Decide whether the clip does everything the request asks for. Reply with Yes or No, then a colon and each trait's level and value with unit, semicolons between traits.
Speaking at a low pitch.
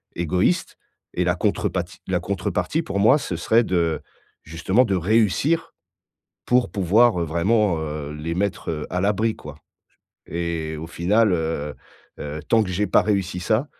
Yes: very low, 90 Hz